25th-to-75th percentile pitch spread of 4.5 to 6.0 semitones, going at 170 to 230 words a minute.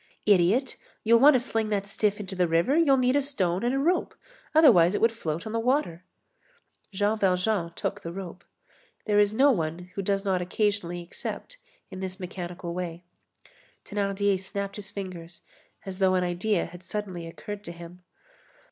No: average, 3.5 semitones; average, 175 wpm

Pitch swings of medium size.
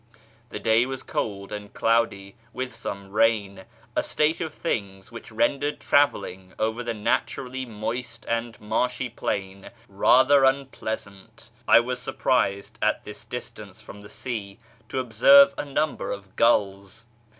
Yes: average, 4.4 semitones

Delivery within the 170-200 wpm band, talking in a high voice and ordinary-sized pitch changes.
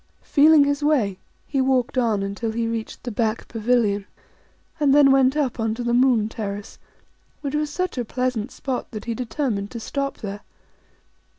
Yes: average, 175 wpm; high, 245 Hz; average, 3.9 semitones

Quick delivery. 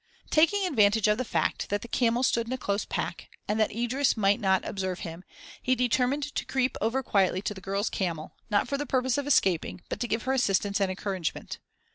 Yes: fast, 215 wpm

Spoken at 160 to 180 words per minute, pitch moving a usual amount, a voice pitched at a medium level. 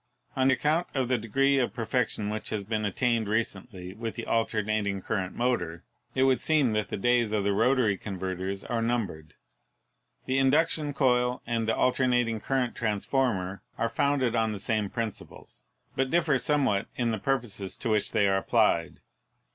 No: average, 170 wpm; average, 4.0 semitones; low, 115 Hz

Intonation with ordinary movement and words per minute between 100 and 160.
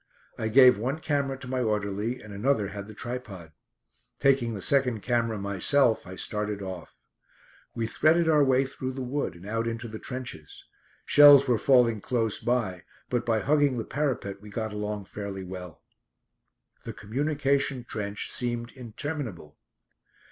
Yes: average, 4.3 semitones; average, 155 wpm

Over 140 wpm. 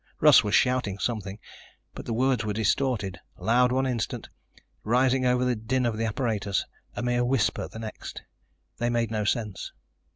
Yes: average, 165 wpm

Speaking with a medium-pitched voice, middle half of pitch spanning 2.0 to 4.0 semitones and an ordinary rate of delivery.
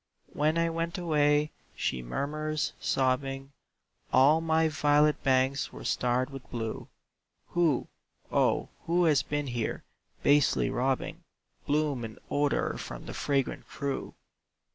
No: medium, 145 Hz; average, 2.8 semitones; slow, 120 wpm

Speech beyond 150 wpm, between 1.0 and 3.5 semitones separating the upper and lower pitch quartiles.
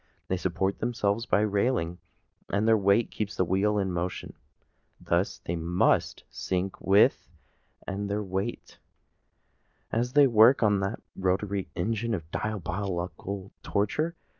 No: slow, 135 wpm; narrow, 2.5 semitones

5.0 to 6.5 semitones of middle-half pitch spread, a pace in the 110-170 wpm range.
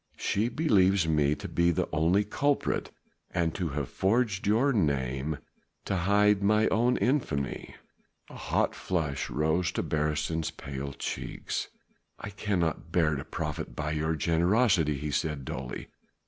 Yes: average, 5.3 semitones; average, 140 wpm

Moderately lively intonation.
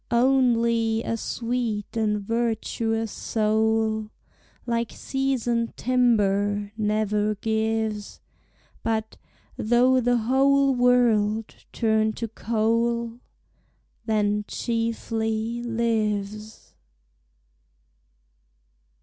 No: narrow, 1.6 semitones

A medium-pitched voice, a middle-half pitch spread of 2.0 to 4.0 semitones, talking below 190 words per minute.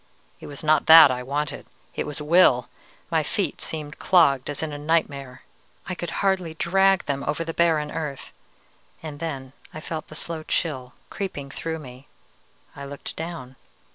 Yes: medium, 155 Hz; average, 3.0 semitones; average, 170 wpm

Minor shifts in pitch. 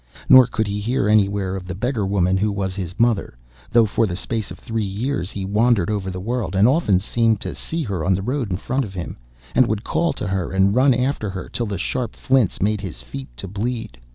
No: average, 3.8 semitones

